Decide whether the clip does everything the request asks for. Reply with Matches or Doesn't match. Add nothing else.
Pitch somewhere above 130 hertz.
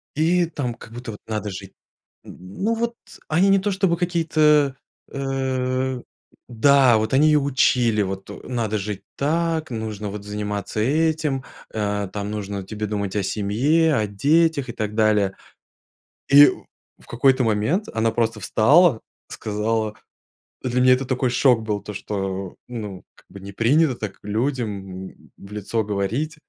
Doesn't match